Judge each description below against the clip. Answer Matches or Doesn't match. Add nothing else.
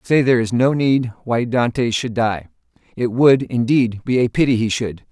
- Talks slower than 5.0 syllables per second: Matches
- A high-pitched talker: Doesn't match